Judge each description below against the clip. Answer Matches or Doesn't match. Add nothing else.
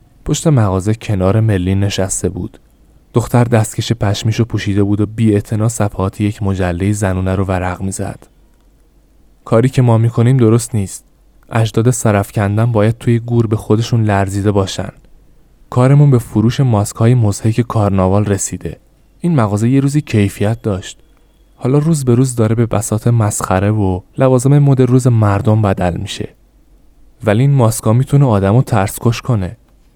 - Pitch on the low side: Matches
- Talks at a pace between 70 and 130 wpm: Doesn't match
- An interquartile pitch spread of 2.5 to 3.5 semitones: Matches